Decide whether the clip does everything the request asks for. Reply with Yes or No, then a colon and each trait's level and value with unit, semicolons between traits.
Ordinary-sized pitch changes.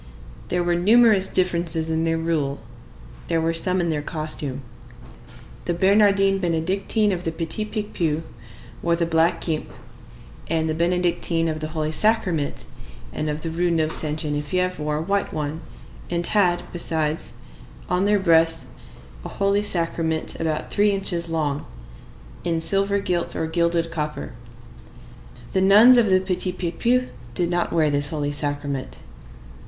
Yes: average, 3.0 semitones